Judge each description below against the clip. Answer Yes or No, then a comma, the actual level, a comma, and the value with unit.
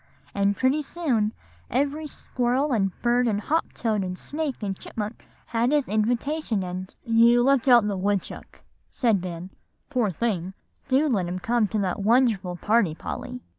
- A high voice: Yes, high, 230 Hz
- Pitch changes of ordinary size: Yes, average, 4.6 semitones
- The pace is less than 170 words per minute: Yes, average, 160 wpm